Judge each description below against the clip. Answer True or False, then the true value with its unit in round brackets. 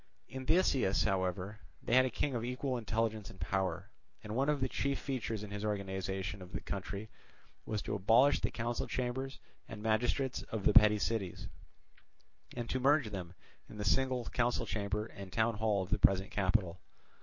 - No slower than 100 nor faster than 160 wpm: False (180 wpm)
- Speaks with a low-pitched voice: True (110 Hz)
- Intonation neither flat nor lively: True (4.1 semitones)